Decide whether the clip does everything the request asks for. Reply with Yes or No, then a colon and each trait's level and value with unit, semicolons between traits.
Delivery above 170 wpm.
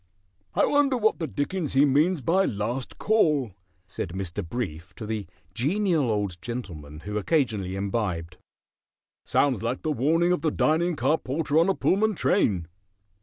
No: average, 155 wpm